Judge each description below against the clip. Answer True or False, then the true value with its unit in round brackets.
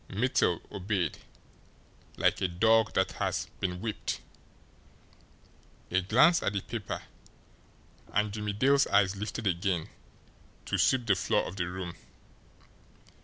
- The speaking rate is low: True (120 wpm)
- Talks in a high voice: False (100 Hz)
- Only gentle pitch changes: False (3.3 semitones)